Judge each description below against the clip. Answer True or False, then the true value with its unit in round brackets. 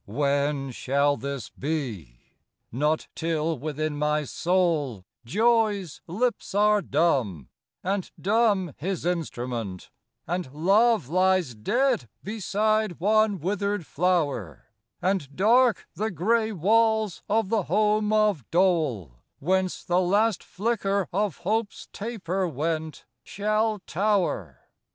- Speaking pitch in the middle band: True (180 Hz)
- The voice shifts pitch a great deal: True (6.3 semitones)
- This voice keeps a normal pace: False (110 wpm)